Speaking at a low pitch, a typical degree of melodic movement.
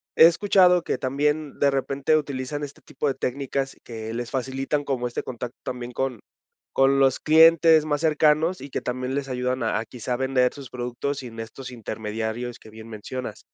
Yes: low, 130 Hz; average, 3.1 semitones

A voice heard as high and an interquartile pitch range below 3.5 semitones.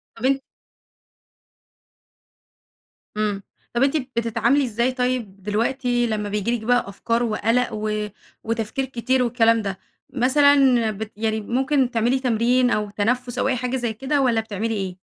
Yes: high, 235 Hz; average, 2.8 semitones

